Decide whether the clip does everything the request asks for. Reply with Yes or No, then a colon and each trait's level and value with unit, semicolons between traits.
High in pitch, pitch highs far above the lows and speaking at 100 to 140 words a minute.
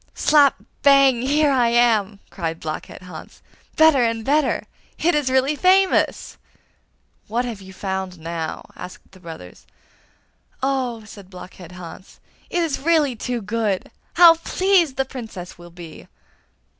Yes: high, 235 Hz; wide, 7.2 semitones; slow, 135 wpm